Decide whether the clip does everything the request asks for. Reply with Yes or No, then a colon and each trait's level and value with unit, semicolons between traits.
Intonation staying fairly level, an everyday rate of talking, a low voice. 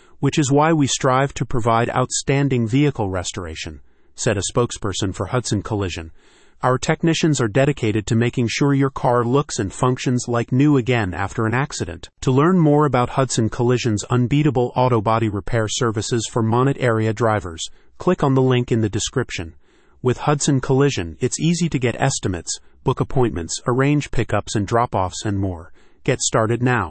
No: average, 4.0 semitones; average, 170 wpm; low, 120 Hz